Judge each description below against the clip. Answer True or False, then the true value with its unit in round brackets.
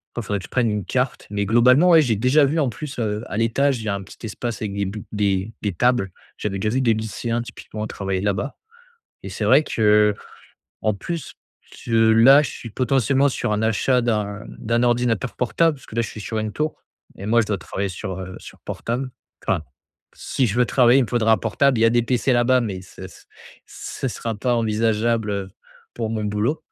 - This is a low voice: True (115 Hz)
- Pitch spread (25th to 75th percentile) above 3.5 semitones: False (3.2 semitones)